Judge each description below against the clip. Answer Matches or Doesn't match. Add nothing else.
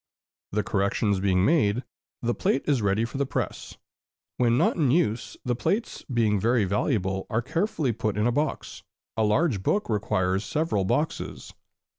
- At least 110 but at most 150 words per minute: Doesn't match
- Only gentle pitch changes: Doesn't match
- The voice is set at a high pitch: Doesn't match